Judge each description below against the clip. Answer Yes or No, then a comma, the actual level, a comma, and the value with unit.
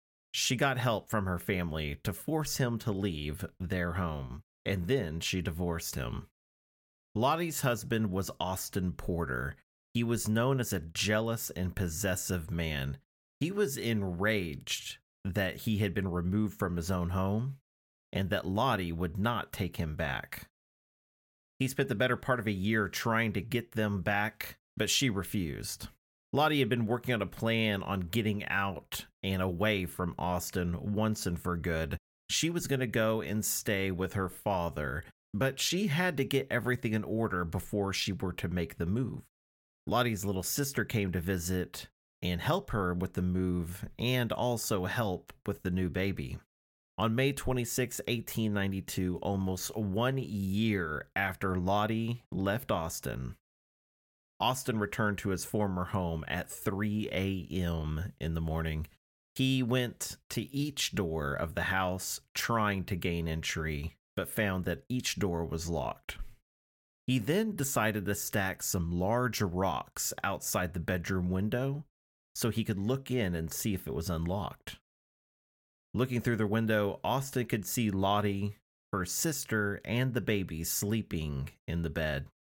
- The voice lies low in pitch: Yes, low, 100 Hz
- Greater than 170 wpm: No, average, 155 wpm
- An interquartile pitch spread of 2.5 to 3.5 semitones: No, average, 4.6 semitones